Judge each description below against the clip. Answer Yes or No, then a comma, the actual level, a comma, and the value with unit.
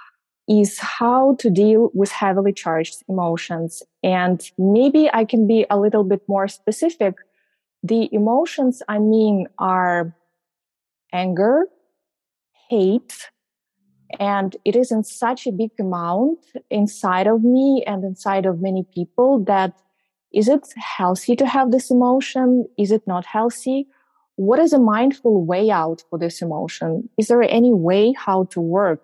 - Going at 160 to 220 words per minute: No, average, 145 wpm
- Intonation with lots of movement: No, average, 4.5 semitones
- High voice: Yes, high, 210 Hz